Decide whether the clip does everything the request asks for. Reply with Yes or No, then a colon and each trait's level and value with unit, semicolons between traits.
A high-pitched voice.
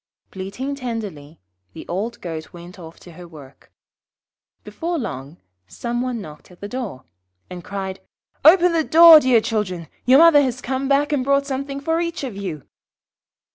Yes: high, 235 Hz